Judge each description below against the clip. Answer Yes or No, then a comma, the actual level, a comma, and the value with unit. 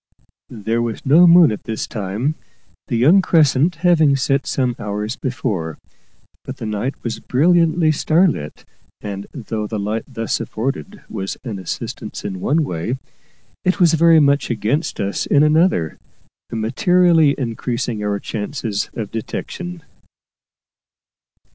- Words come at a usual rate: No, slow, 130 wpm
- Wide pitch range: Yes, wide, 6.8 semitones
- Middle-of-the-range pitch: No, low, 130 Hz